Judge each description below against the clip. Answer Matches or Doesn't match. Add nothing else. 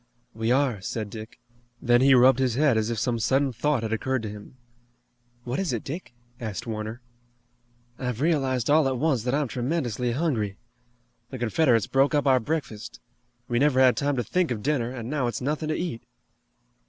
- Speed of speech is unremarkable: Matches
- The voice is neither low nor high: Doesn't match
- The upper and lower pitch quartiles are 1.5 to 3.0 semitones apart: Doesn't match